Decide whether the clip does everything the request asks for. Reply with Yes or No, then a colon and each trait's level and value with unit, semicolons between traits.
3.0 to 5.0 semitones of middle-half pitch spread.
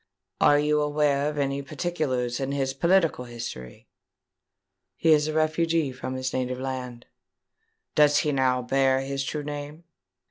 No: narrow, 2.5 semitones